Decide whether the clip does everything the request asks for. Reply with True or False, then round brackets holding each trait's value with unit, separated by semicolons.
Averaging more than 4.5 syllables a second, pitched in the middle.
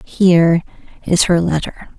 False (4.1 syllables/s; 170 Hz)